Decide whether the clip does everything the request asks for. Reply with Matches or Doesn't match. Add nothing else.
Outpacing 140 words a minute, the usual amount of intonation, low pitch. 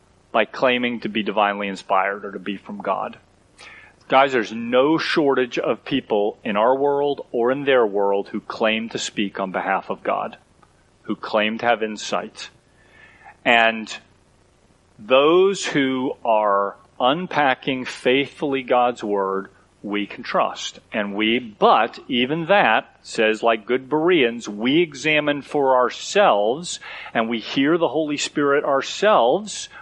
Doesn't match